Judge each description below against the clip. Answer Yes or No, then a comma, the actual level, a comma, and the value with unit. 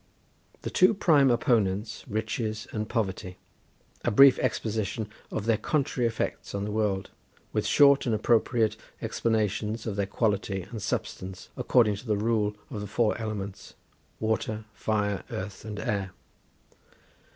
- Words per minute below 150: Yes, average, 140 wpm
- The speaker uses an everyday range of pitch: No, narrow, 2.2 semitones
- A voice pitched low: Yes, low, 110 Hz